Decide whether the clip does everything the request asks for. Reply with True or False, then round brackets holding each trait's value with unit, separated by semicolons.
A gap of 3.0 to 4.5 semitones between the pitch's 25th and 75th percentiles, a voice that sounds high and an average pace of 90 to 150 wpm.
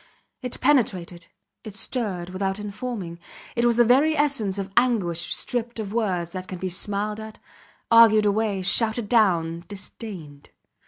True (4.0 semitones; 210 Hz; 145 wpm)